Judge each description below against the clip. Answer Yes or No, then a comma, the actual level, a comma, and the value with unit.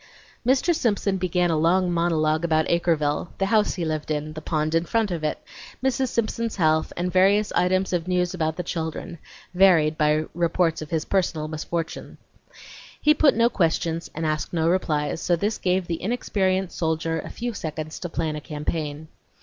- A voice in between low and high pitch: Yes, medium, 170 Hz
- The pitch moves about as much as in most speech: Yes, average, 3.1 semitones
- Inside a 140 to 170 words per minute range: No, average, 180 wpm